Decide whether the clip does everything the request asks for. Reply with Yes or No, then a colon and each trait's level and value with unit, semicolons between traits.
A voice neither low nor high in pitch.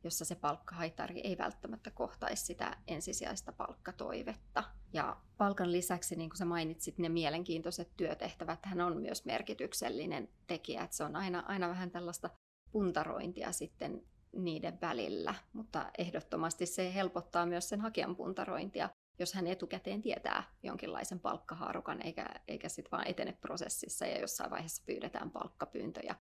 Yes: medium, 175 Hz